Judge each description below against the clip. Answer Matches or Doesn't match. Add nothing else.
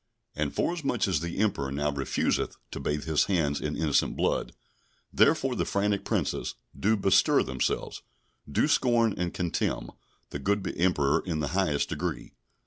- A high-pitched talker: Doesn't match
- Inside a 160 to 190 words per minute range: Doesn't match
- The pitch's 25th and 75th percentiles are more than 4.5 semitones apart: Matches